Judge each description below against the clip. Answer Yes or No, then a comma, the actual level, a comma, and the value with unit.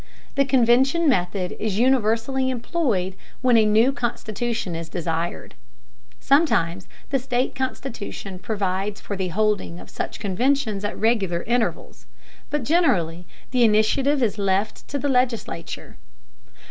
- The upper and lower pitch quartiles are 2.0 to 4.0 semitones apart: No, average, 5.3 semitones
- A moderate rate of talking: No, slow, 125 wpm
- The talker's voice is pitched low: No, high, 225 Hz